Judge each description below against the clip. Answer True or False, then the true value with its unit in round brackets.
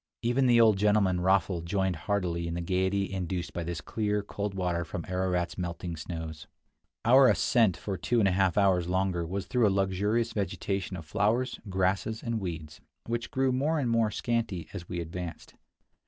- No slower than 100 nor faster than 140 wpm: False (180 wpm)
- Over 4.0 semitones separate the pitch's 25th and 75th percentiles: False (3.6 semitones)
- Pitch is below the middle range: True (95 Hz)